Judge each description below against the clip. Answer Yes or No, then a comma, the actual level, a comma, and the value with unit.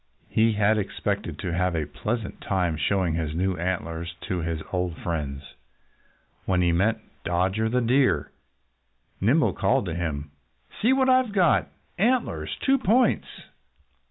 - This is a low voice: Yes, very low, 95 Hz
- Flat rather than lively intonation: No, wide, 5.5 semitones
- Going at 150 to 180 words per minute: No, average, 140 wpm